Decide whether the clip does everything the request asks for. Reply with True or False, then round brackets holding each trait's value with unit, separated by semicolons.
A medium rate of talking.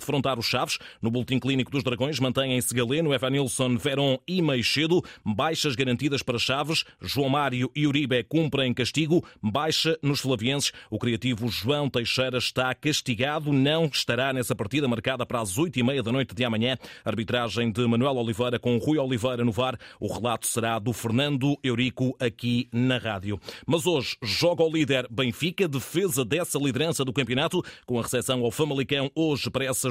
True (170 wpm)